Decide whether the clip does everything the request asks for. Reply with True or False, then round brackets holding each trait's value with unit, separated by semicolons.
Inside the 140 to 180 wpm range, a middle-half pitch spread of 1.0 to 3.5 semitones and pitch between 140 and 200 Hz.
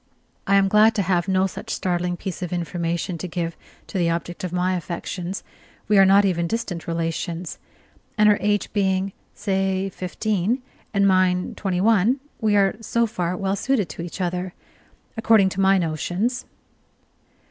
True (165 wpm; 2.4 semitones; 190 Hz)